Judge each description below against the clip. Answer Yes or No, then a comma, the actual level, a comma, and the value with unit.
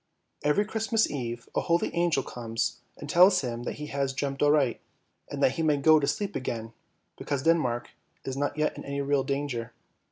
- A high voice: No, medium, 140 Hz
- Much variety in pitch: No, average, 3.8 semitones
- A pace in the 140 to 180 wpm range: No, average, 190 wpm